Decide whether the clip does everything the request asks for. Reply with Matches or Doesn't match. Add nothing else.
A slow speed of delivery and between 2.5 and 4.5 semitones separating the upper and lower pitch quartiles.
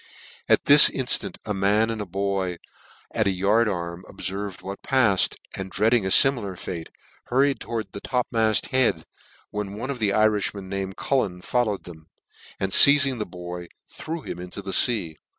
Doesn't match